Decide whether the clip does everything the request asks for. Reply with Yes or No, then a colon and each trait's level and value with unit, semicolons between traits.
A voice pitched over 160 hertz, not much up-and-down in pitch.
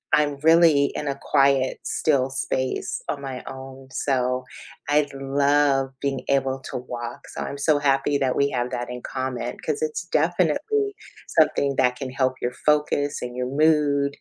No: medium, 140 Hz; narrow, 2.0 semitones